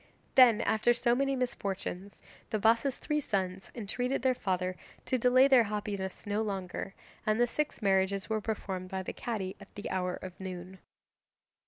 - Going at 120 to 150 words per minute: No, average, 165 wpm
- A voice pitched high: Yes, high, 210 Hz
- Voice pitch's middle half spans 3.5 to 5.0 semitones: Yes, average, 4.2 semitones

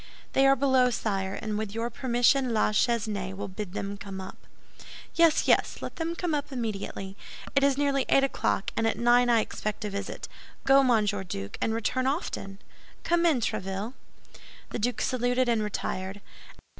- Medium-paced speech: Yes, average, 170 wpm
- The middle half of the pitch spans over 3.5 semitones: Yes, average, 4.6 semitones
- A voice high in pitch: Yes, high, 230 Hz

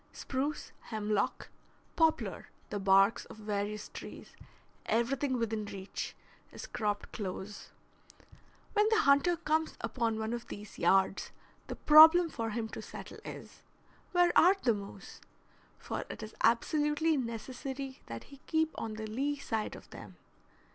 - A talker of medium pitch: No, high, 235 Hz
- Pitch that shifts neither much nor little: No, wide, 5.9 semitones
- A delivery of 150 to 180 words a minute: No, average, 140 wpm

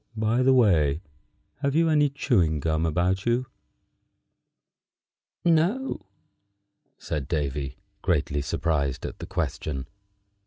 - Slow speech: Yes, slow, 105 wpm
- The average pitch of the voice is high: No, very low, 90 Hz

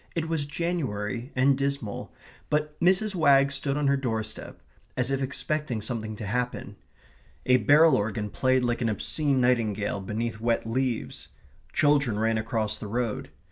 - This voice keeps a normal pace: Yes, average, 150 wpm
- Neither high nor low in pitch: No, low, 125 Hz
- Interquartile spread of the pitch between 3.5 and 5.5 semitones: Yes, average, 4.3 semitones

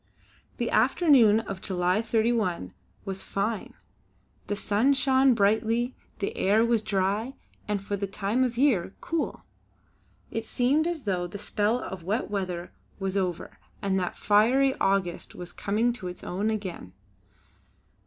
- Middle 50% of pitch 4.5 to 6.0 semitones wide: No, average, 3.8 semitones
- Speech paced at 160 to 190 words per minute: No, average, 145 wpm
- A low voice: No, high, 210 Hz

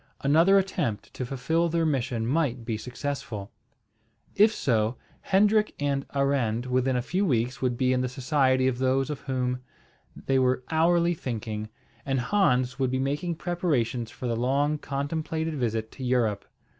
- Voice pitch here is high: No, low, 130 Hz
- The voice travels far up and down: No, average, 3.9 semitones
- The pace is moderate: Yes, average, 155 wpm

